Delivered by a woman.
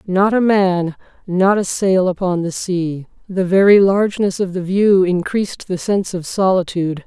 Yes: female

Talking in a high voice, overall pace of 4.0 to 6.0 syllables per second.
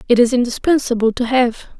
Yes: high, 245 Hz; 5.9 syllables/s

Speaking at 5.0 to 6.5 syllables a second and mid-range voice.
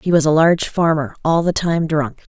Yes: 5.1 syllables/s; medium, 160 Hz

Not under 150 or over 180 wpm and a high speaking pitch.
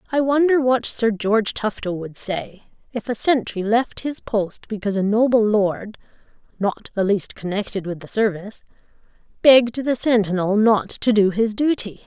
Yes: average, 165 wpm; high, 220 Hz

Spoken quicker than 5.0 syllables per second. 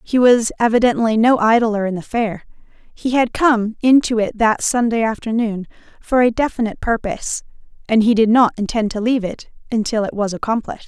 Yes: 5.5 syllables/s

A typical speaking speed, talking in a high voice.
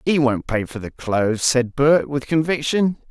No: average, 195 wpm; low, 135 Hz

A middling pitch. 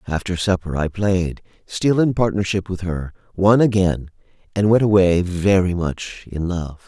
No: very low, 95 Hz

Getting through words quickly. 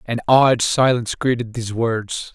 No: average, 155 wpm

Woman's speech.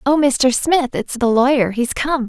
Yes: female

